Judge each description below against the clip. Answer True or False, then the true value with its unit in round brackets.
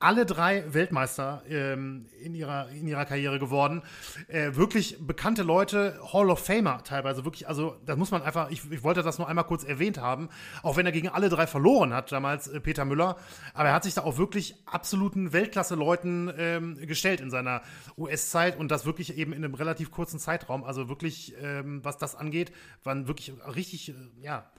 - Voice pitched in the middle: True (160 Hz)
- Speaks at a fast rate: True (195 wpm)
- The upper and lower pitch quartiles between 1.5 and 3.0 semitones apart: False (3.6 semitones)